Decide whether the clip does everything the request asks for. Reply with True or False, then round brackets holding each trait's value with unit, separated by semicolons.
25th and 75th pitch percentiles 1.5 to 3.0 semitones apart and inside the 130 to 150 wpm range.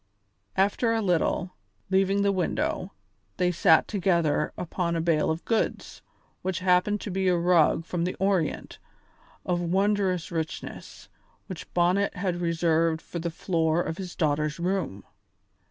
True (2.5 semitones; 140 wpm)